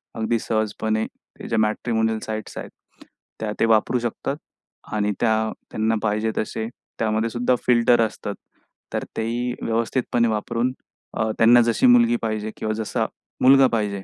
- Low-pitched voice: Yes, low, 110 Hz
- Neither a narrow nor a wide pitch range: No, narrow, 1.6 semitones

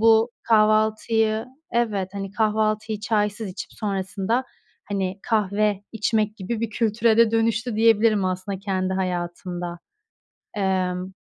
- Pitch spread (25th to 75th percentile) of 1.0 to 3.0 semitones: Yes, average, 2.7 semitones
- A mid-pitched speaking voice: No, high, 210 Hz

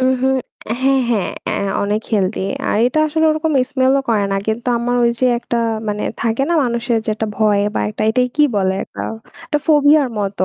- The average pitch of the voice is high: Yes, high, 235 Hz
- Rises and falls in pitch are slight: No, average, 4.3 semitones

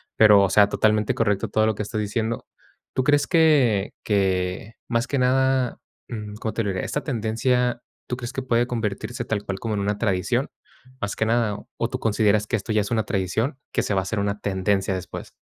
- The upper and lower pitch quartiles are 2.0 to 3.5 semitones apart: Yes, average, 2.9 semitones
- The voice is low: Yes, low, 110 Hz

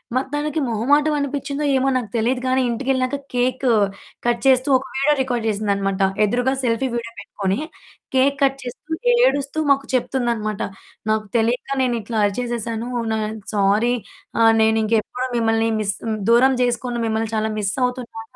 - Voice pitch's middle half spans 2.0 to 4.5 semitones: Yes, average, 3.0 semitones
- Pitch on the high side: Yes, high, 240 Hz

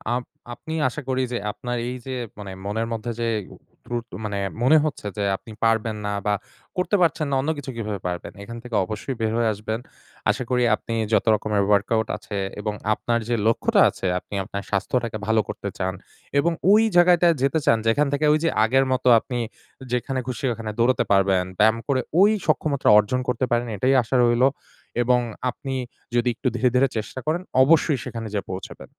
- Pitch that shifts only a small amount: No, average, 3.8 semitones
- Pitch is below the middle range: Yes, low, 120 Hz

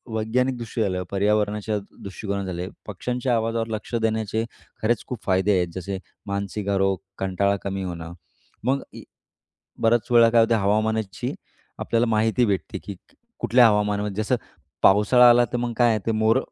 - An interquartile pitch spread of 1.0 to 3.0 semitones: Yes, average, 2.7 semitones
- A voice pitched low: Yes, low, 110 Hz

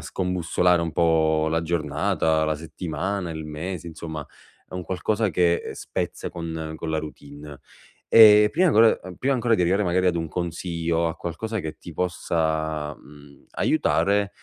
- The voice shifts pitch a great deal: No, average, 2.7 semitones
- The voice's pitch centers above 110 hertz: No, very low, 85 Hz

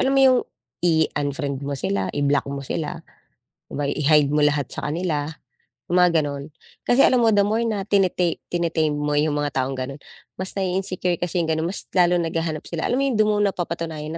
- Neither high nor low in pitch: Yes, medium, 165 Hz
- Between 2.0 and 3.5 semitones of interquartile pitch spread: No, average, 4.3 semitones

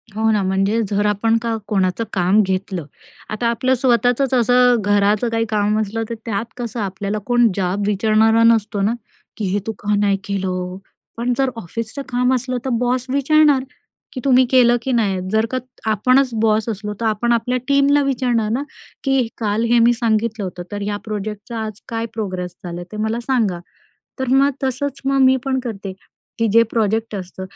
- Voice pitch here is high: Yes, high, 225 Hz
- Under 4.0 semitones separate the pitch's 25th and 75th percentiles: Yes, average, 3.3 semitones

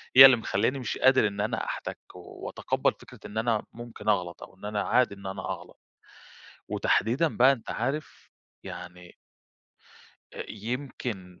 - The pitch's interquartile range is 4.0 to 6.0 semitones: Yes, average, 4.4 semitones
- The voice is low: Yes, low, 110 Hz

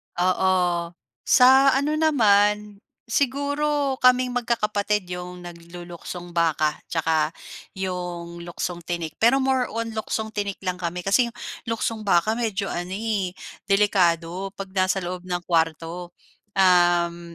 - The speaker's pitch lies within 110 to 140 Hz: No, high, 190 Hz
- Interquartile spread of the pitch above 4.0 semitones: Yes, average, 4.4 semitones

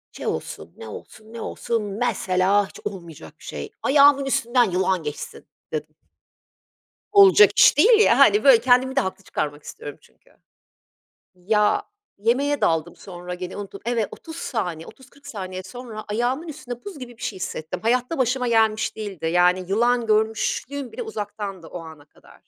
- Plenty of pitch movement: Yes, wide, 5.8 semitones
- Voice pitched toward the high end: Yes, high, 220 Hz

